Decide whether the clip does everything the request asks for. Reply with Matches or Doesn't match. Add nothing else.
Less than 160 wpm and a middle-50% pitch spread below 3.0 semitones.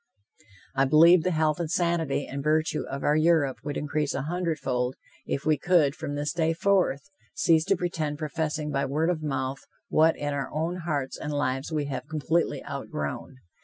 Doesn't match